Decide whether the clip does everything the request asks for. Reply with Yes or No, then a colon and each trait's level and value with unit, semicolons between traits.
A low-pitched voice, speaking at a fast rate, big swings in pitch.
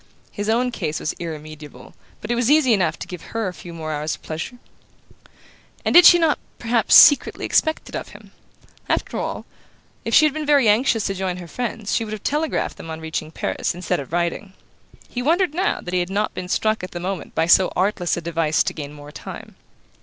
No: high, 190 Hz; fast, 220 wpm; wide, 6.8 semitones